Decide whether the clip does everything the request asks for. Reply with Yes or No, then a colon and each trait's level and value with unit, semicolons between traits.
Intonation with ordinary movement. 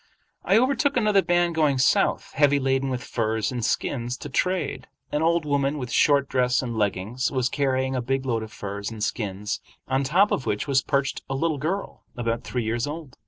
Yes: average, 4.0 semitones